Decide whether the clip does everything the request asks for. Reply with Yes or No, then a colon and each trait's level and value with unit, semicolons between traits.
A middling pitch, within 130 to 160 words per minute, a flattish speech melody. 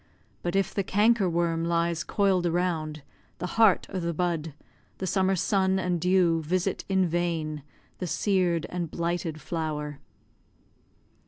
Yes: medium, 175 Hz; average, 140 wpm; narrow, 2.3 semitones